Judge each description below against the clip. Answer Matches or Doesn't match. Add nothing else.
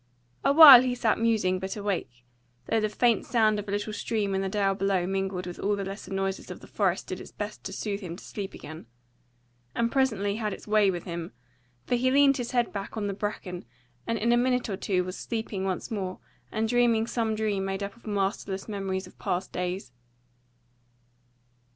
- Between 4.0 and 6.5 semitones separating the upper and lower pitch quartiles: Doesn't match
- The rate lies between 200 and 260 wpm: Matches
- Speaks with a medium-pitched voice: Doesn't match